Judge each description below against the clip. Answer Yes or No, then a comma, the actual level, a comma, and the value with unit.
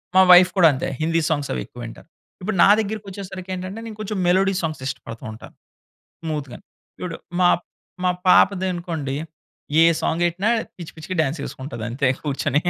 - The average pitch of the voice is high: No, medium, 170 Hz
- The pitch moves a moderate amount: Yes, average, 4.7 semitones